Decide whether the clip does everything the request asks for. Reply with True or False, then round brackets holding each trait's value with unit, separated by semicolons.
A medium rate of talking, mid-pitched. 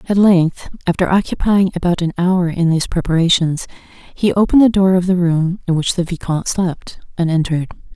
True (180 wpm; 175 Hz)